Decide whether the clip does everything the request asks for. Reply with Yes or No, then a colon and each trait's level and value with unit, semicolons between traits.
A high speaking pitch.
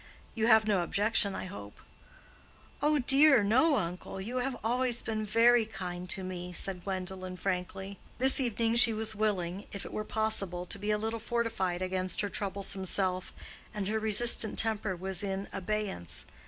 Yes: high, 205 Hz